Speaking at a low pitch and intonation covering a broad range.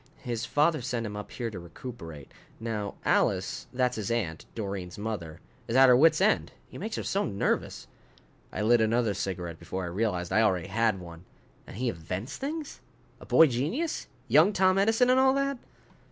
Yes: low, 115 Hz; wide, 8.3 semitones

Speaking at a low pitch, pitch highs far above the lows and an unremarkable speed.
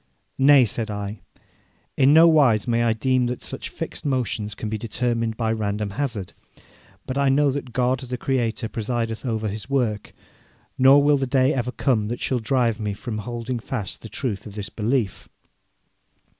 No: low, 120 Hz; average, 3.3 semitones; average, 175 wpm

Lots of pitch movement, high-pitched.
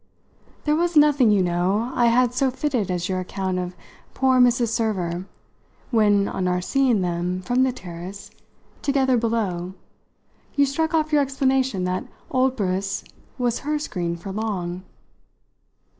Yes: wide, 6.3 semitones; high, 220 Hz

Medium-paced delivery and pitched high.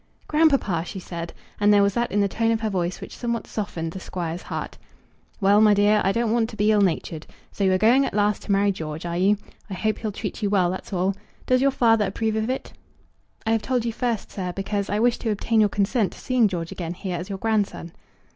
No: fast, 245 wpm; high, 205 Hz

